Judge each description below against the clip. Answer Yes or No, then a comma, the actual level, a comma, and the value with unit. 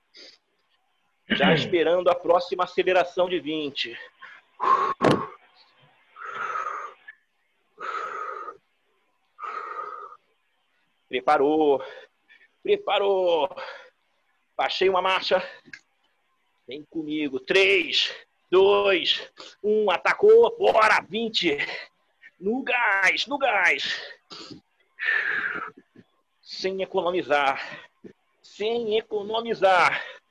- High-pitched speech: Yes, high, 230 Hz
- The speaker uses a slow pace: Yes, slow, 55 wpm